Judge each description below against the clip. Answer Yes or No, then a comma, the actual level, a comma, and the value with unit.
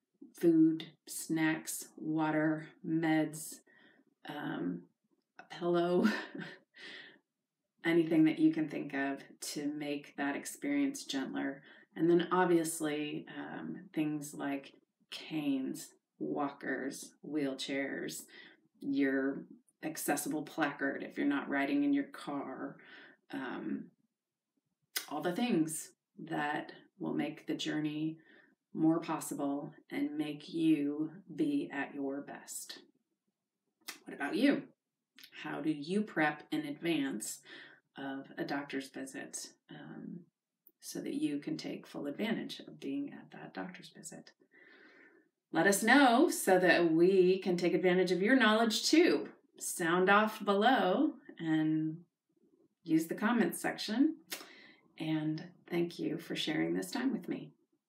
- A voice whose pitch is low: No, medium, 180 Hz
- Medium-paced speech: No, slow, 115 wpm